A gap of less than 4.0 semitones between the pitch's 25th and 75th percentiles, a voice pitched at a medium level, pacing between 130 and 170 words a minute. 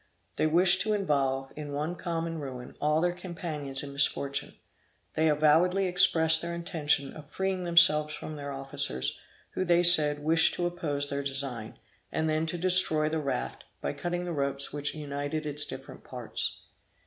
Yes: average, 3.4 semitones; medium, 155 Hz; average, 165 wpm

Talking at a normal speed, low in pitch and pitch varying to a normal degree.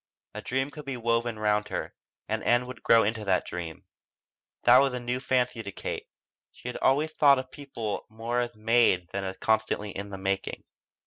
Yes: average, 195 wpm; low, 115 Hz; average, 3.4 semitones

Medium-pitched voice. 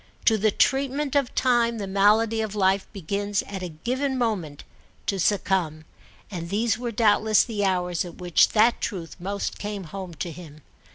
No: high, 200 Hz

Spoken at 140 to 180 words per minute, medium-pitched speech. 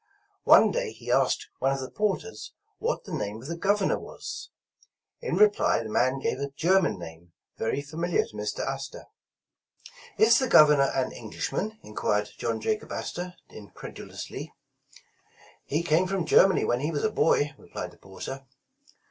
Yes: average, 160 wpm; medium, 145 Hz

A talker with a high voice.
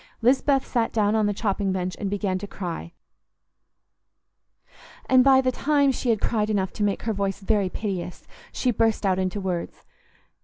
Yes: high, 205 Hz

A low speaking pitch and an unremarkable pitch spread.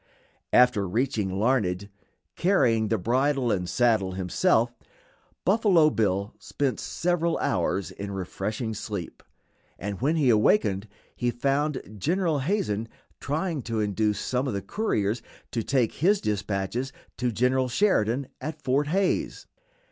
No: low, 120 Hz; wide, 5.9 semitones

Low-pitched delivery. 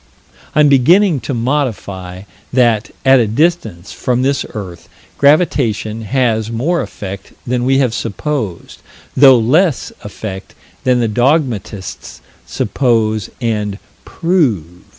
Yes: low, 120 Hz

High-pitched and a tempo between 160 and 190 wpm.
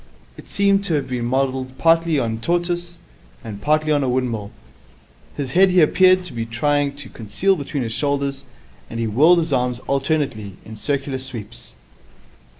No: low, 135 Hz; average, 170 wpm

